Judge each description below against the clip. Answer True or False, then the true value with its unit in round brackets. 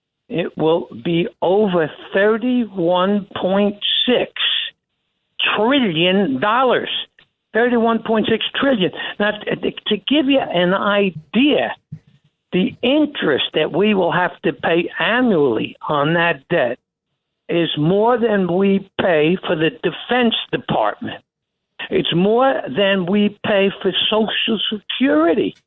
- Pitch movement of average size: True (4.8 semitones)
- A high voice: True (200 Hz)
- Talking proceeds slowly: True (105 wpm)